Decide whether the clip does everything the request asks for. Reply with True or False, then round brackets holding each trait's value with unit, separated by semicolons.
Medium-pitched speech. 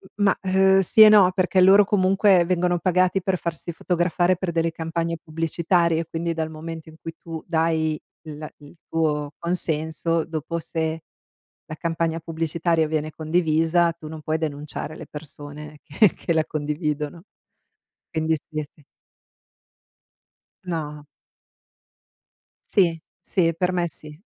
True (165 Hz)